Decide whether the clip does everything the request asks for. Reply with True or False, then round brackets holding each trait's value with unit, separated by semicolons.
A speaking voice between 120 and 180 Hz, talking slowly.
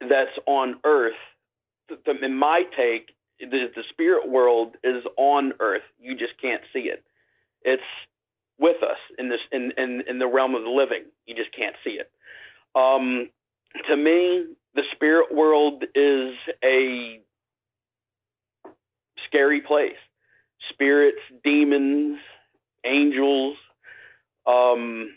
True (140 Hz; 125 wpm)